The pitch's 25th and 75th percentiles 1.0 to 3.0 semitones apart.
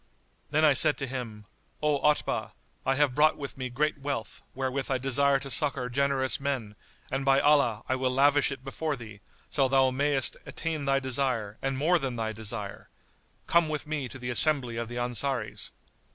Yes: narrow, 2.5 semitones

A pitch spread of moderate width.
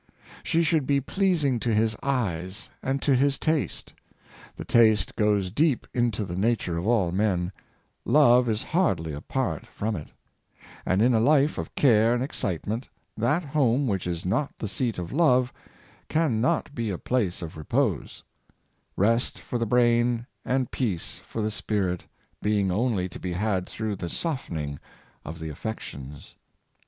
No: wide, 5.7 semitones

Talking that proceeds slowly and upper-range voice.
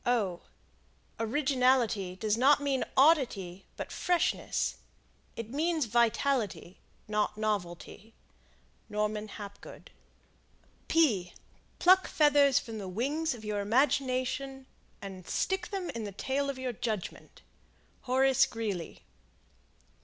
Yes: slow, 100 wpm; high, 240 Hz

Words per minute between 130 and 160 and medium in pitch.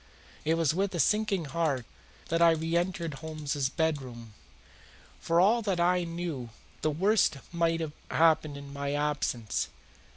Yes: average, 140 wpm; medium, 160 Hz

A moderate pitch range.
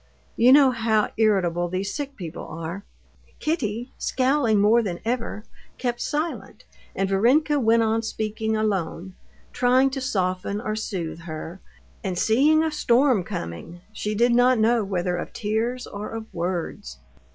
Yes: average, 4.8 semitones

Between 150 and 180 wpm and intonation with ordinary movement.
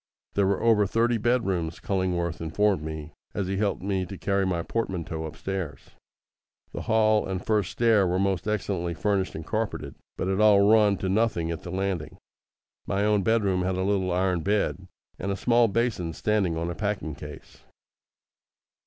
Yes: average, 170 wpm; average, 3.1 semitones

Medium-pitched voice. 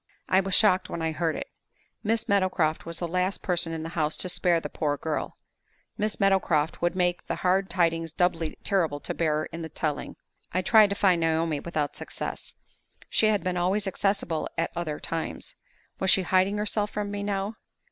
Yes: medium, 180 Hz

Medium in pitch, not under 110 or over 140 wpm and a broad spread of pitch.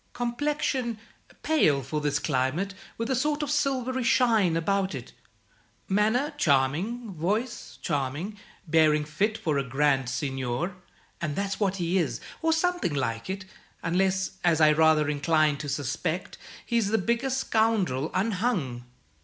Yes: medium, 180 Hz; slow, 135 wpm; wide, 7.7 semitones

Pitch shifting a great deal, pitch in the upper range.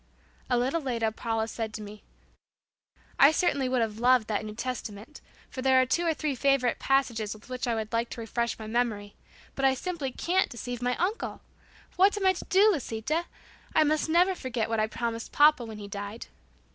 No: average, 4.7 semitones; high, 245 Hz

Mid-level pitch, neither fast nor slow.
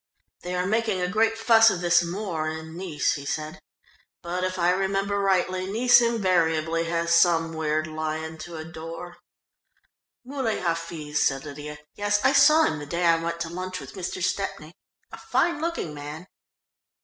Yes: medium, 175 Hz; average, 165 wpm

